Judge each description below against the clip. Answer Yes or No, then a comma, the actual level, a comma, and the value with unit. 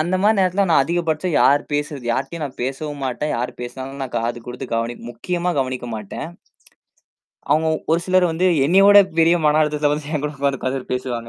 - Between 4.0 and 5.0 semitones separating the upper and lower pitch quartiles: Yes, average, 4.7 semitones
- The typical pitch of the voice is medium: Yes, medium, 150 Hz